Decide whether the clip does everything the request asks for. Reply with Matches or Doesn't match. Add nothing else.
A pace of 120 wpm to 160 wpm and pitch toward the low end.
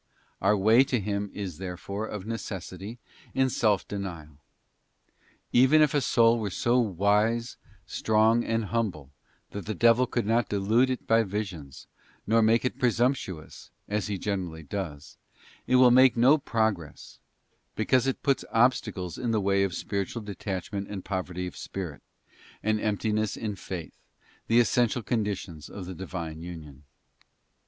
Matches